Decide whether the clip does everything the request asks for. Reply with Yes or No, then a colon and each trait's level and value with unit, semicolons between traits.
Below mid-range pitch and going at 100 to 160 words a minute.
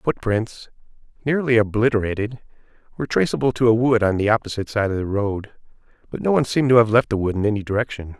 No: low, 110 Hz; average, 200 wpm